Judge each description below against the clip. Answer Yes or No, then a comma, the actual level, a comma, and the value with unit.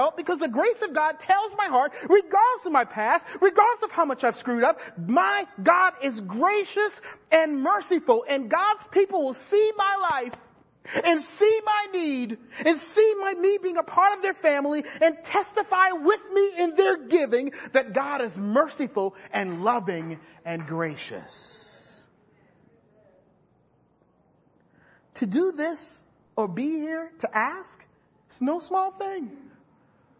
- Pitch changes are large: Yes, wide, 6.9 semitones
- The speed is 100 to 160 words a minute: Yes, average, 145 wpm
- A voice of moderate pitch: No, very high, 330 Hz